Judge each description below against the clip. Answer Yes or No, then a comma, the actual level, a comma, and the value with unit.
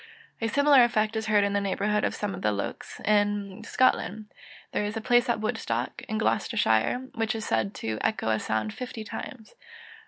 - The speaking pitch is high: Yes, high, 210 Hz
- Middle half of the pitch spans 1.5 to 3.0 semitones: Yes, narrow, 2.5 semitones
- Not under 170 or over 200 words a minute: Yes, average, 190 wpm